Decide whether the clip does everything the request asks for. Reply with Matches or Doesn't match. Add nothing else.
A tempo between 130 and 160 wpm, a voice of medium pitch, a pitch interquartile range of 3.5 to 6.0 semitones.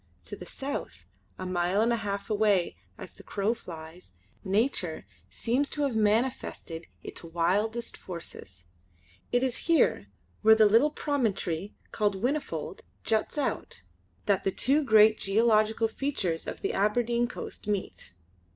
Doesn't match